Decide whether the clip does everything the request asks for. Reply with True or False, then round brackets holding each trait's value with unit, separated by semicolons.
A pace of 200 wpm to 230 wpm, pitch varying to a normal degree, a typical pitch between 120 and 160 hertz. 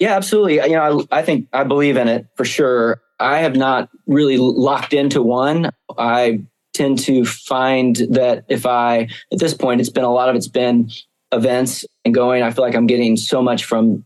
False (205 wpm; 2.3 semitones; 125 Hz)